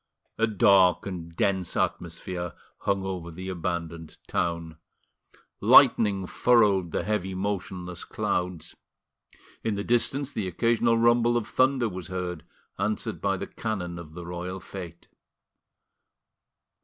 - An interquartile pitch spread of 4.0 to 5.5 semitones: No, average, 3.6 semitones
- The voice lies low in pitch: Yes, very low, 95 Hz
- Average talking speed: No, slow, 120 wpm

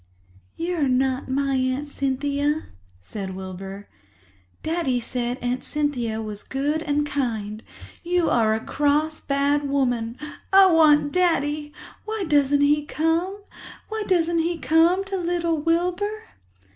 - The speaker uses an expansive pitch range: No, average, 4.4 semitones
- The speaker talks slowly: Yes, slow, 125 wpm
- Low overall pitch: No, very high, 290 Hz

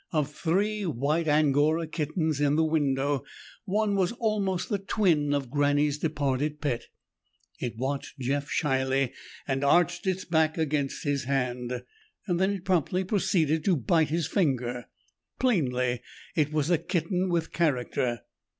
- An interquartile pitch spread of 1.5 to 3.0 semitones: No, average, 4.1 semitones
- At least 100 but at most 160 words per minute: Yes, average, 140 wpm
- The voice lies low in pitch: No, medium, 150 Hz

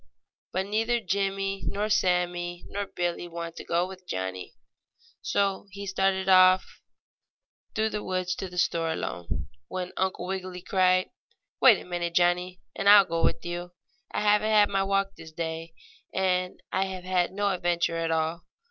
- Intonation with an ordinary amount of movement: No, narrow, 2.0 semitones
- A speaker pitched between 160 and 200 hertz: Yes, medium, 185 Hz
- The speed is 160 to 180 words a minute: Yes, average, 165 wpm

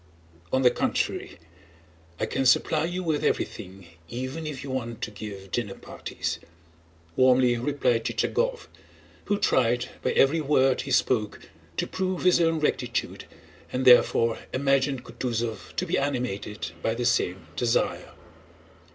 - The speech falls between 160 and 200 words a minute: No, slow, 135 wpm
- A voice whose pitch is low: Yes, low, 130 Hz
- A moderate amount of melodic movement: Yes, average, 4.2 semitones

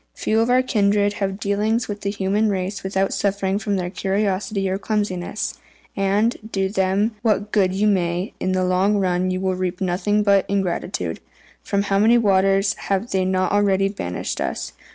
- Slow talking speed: No, average, 180 wpm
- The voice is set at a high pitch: Yes, high, 195 Hz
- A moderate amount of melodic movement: No, narrow, 1.6 semitones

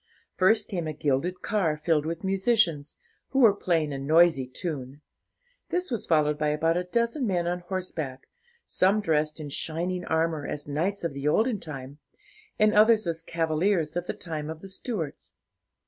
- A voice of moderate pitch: Yes, medium, 165 Hz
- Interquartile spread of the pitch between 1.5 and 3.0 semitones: No, average, 4.2 semitones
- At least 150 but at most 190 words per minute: Yes, average, 170 wpm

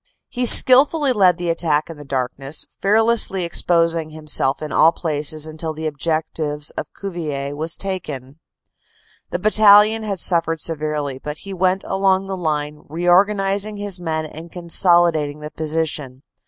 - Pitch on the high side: No, medium, 165 Hz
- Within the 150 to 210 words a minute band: No, average, 140 wpm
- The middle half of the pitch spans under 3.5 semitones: No, average, 4.2 semitones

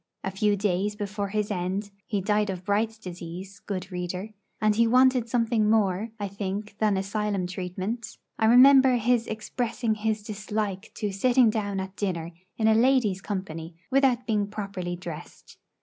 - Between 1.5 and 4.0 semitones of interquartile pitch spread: Yes, narrow, 2.6 semitones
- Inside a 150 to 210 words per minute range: Yes, average, 160 wpm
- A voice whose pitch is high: Yes, high, 210 Hz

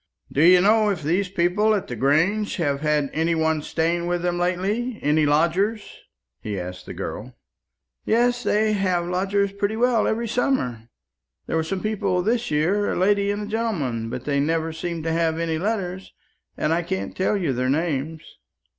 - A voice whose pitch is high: No, medium, 175 Hz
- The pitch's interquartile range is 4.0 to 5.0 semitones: Yes, average, 4.6 semitones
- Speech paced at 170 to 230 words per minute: Yes, average, 180 wpm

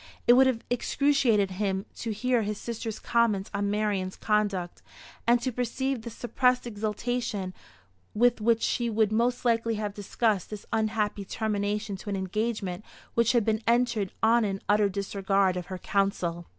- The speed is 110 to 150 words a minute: No, average, 160 wpm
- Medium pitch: No, high, 215 Hz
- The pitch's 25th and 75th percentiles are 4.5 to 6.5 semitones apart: No, average, 2.8 semitones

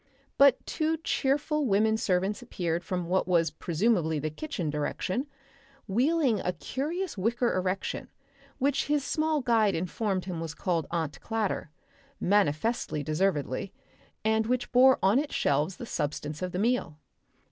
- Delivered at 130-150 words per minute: Yes, average, 140 wpm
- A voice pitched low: No, high, 200 Hz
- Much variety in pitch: Yes, wide, 6.9 semitones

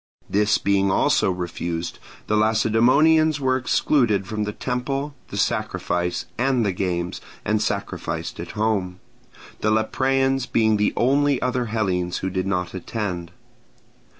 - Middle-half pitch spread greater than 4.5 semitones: Yes, average, 5.1 semitones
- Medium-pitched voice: No, low, 110 Hz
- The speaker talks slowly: Yes, slow, 130 wpm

